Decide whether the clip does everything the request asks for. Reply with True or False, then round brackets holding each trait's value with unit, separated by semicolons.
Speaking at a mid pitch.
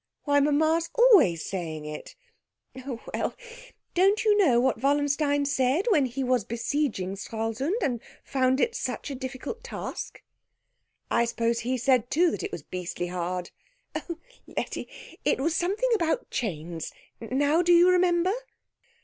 False (275 Hz)